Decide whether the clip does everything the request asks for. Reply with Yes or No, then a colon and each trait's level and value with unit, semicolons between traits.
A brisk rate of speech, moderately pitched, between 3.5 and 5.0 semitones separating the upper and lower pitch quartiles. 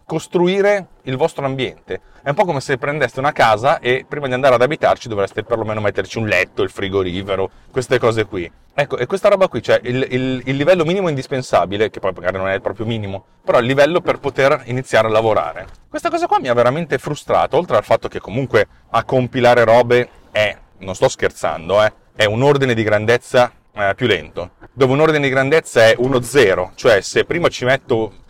No: fast, 200 wpm; low, 125 Hz; average, 4.5 semitones